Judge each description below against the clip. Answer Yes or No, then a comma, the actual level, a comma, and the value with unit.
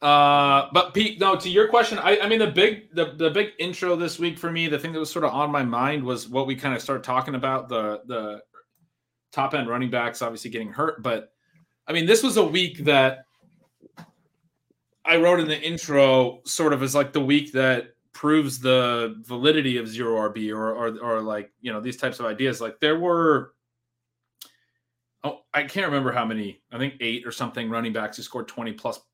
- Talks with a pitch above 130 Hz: Yes, medium, 140 Hz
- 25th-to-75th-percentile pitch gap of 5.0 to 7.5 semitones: Yes, wide, 5.4 semitones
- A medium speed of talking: No, fast, 210 wpm